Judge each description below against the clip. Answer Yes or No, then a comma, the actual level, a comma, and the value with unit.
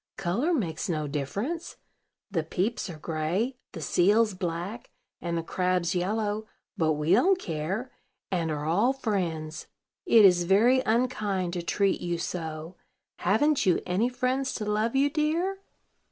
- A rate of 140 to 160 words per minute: Yes, average, 145 wpm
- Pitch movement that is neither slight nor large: No, wide, 5.8 semitones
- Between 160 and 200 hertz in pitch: Yes, high, 190 Hz